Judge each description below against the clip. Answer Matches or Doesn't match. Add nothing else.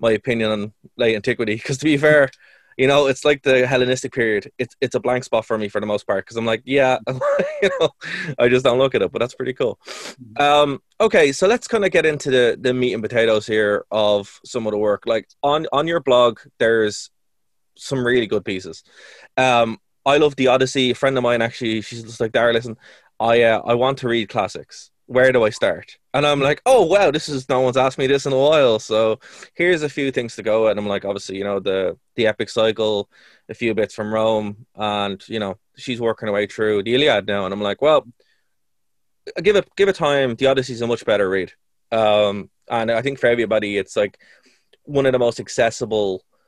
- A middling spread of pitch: Matches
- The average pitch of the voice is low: Matches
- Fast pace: Matches